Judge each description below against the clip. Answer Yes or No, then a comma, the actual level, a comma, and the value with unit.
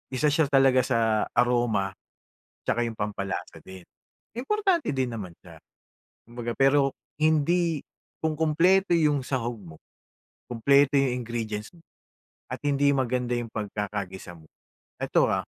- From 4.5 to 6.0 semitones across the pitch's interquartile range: Yes, average, 4.9 semitones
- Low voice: Yes, low, 125 Hz